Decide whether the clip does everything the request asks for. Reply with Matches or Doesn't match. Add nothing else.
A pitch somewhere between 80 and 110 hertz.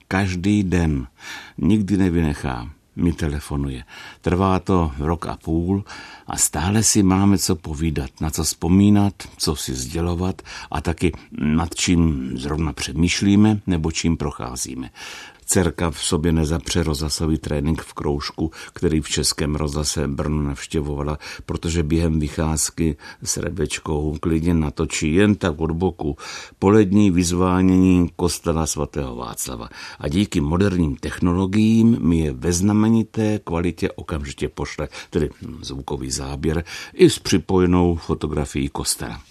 Matches